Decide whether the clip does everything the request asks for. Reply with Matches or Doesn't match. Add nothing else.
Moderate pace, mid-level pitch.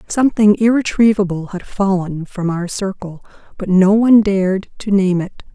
Doesn't match